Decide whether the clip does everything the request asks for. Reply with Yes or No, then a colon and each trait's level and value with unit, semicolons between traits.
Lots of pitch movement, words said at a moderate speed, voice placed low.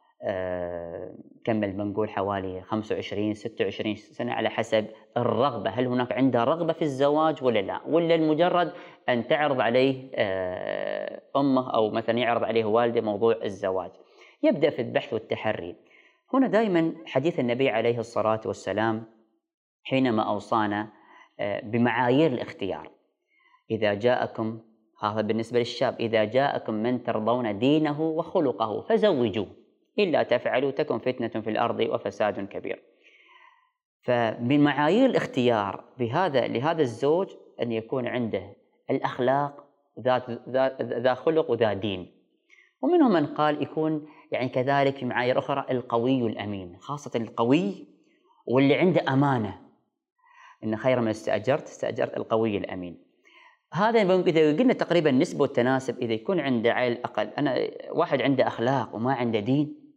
Yes: wide, 6.1 semitones; average, 120 wpm; low, 125 Hz